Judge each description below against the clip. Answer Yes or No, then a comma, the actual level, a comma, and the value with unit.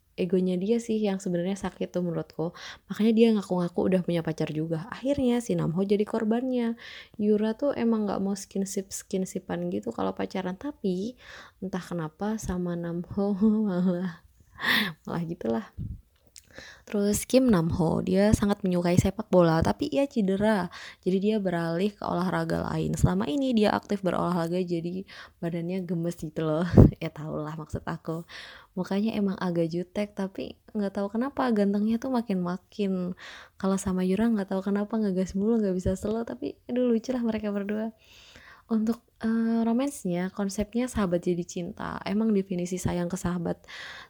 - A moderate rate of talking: No, fast, 150 wpm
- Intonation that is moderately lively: Yes, average, 3.6 semitones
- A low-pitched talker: No, high, 195 Hz